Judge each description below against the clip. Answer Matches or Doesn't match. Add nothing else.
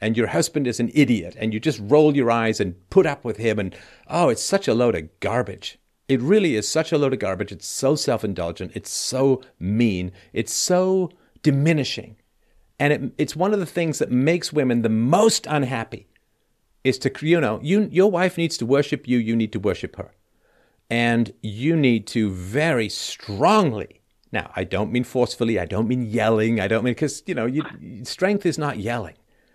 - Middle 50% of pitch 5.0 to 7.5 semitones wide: Matches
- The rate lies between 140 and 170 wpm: Doesn't match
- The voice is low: Matches